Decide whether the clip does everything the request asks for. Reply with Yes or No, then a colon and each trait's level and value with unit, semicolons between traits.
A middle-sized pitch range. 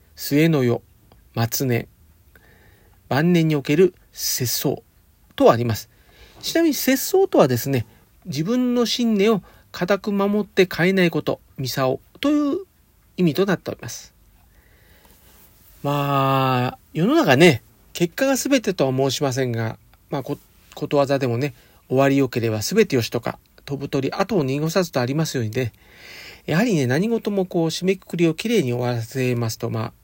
No: wide, 8.1 semitones